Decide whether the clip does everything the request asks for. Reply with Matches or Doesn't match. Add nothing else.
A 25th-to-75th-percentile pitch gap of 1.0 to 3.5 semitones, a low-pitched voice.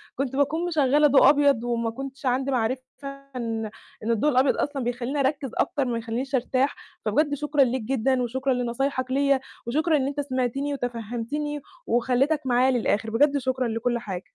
Doesn't match